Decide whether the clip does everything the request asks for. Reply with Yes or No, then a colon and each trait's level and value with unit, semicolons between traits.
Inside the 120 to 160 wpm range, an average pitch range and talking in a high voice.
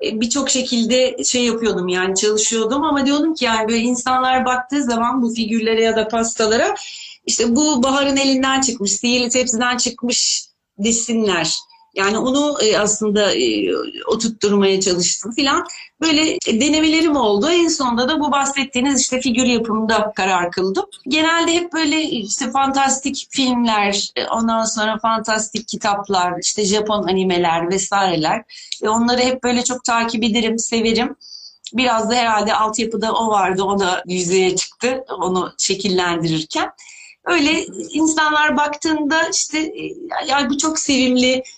Yes: average, 130 wpm; average, 4.8 semitones; high, 245 Hz